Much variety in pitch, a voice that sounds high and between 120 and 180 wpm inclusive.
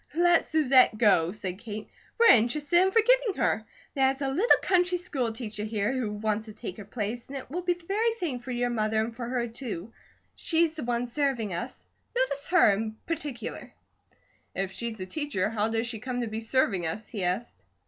No: wide, 5.9 semitones; high, 240 Hz; average, 200 wpm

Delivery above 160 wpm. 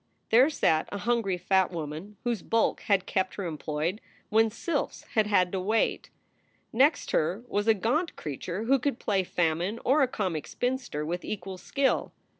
Yes: average, 170 wpm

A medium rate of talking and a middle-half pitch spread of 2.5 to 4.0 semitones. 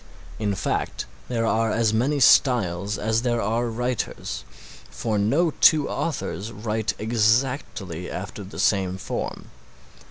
No: slow, 125 wpm; average, 3.0 semitones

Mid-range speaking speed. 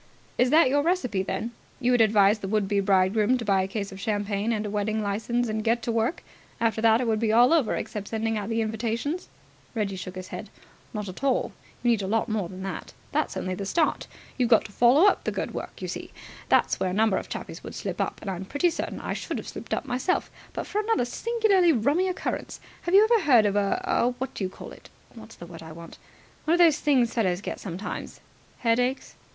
No: fast, 235 wpm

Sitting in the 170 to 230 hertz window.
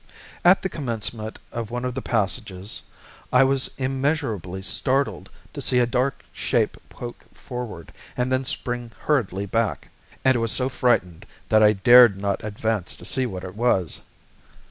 No: low, 120 Hz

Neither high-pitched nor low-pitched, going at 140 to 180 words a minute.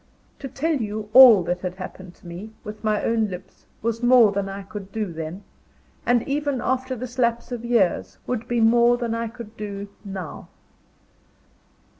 No: high, 220 Hz; average, 175 wpm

